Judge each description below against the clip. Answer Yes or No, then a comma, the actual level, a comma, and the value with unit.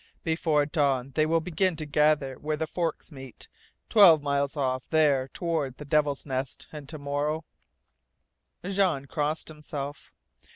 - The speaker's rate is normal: Yes, average, 150 wpm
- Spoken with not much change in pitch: Yes, narrow, 2.2 semitones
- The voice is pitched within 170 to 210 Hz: No, medium, 150 Hz